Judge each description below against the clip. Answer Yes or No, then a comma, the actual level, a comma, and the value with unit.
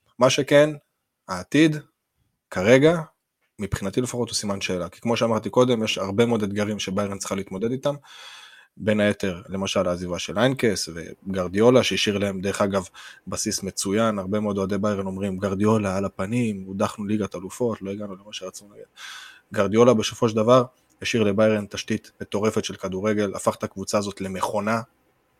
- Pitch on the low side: Yes, low, 105 Hz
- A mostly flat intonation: No, average, 3.1 semitones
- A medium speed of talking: No, fast, 155 wpm